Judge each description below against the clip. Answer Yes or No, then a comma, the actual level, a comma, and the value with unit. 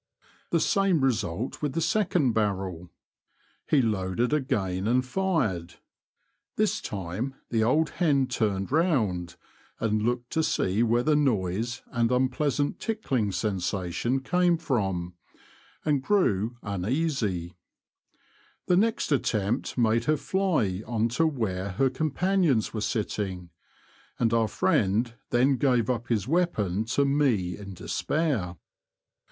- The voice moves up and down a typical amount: No, wide, 6.5 semitones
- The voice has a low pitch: Yes, low, 120 Hz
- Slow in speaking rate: Yes, slow, 125 wpm